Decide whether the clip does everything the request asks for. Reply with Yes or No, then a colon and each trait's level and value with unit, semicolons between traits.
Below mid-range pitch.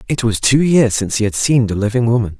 Yes: low, 115 Hz